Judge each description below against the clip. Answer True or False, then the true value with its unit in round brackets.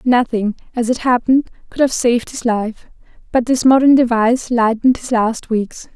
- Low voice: False (240 Hz)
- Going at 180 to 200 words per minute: False (170 wpm)